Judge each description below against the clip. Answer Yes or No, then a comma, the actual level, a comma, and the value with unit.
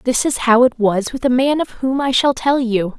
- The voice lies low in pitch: No, very high, 250 Hz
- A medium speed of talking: No, fast, 280 wpm